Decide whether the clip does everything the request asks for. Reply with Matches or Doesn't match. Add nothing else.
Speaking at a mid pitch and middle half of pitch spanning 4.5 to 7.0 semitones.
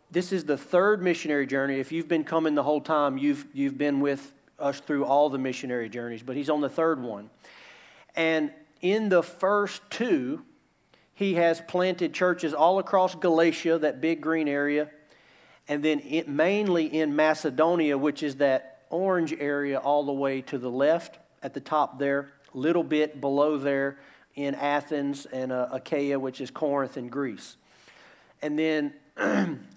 Doesn't match